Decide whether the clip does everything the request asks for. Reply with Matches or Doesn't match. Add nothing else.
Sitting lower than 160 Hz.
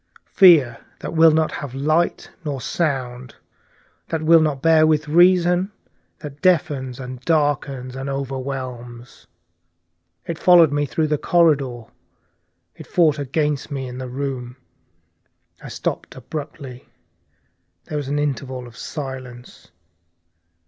Matches